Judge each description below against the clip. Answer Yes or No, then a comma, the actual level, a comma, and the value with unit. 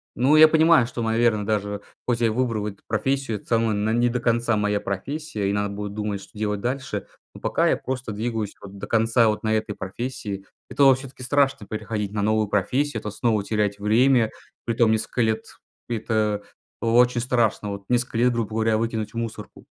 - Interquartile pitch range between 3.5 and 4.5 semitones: No, average, 2.7 semitones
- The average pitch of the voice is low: Yes, low, 110 Hz